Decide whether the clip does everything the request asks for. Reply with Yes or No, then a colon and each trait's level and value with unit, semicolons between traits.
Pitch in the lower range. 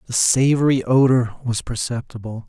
Yes: low, 120 Hz